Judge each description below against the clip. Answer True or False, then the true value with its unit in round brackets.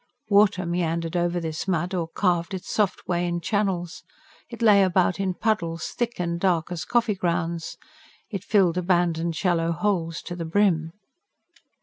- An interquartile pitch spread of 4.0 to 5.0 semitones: False (2.7 semitones)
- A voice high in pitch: False (175 Hz)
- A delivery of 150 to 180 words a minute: True (155 wpm)